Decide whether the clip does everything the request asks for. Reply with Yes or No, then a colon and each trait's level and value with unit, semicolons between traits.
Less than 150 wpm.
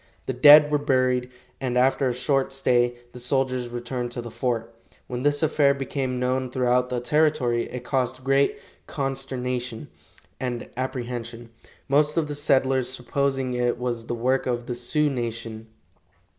No: average, 155 wpm